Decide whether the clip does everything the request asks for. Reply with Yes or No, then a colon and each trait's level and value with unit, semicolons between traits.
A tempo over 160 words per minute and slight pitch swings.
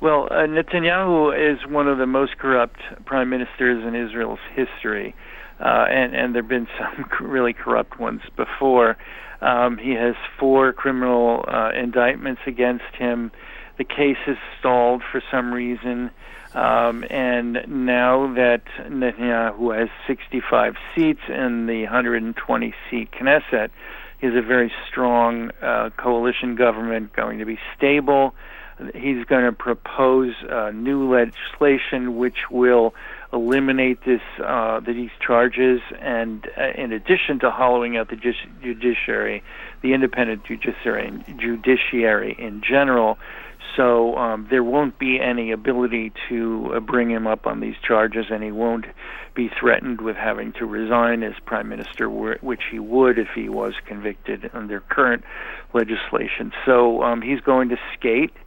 No: average, 145 wpm; narrow, 1.9 semitones